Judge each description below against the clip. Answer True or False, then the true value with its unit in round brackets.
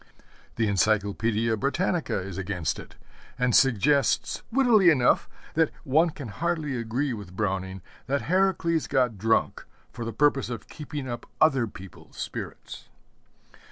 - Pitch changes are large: True (6.1 semitones)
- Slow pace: True (130 wpm)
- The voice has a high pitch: False (125 Hz)